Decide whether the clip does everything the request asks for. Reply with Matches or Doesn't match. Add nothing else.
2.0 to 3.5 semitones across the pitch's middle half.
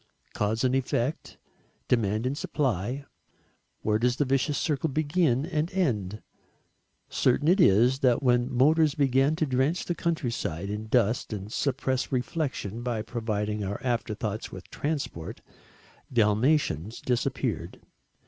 Doesn't match